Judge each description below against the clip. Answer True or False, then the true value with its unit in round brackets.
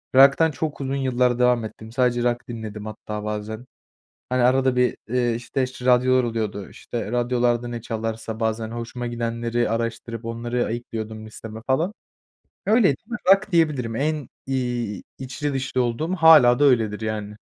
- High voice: False (120 Hz)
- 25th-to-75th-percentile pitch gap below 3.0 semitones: True (2.5 semitones)